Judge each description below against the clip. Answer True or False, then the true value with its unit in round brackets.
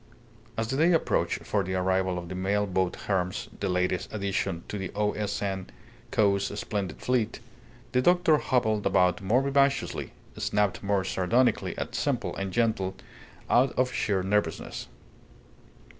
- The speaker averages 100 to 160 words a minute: True (150 wpm)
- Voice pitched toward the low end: True (100 Hz)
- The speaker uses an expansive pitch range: False (3.7 semitones)